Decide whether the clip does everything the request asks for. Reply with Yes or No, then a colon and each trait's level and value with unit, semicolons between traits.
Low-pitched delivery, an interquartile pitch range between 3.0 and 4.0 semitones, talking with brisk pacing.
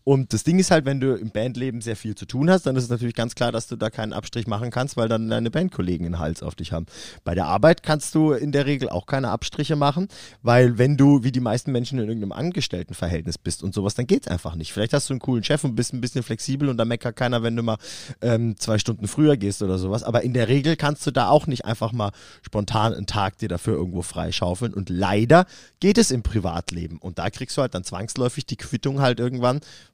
No: low, 120 Hz; average, 4.8 semitones; fast, 250 wpm